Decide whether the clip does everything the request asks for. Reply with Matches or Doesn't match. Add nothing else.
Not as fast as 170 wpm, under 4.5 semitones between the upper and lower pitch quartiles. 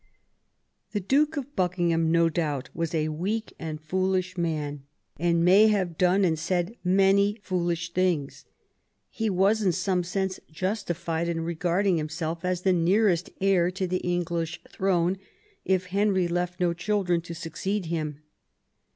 Matches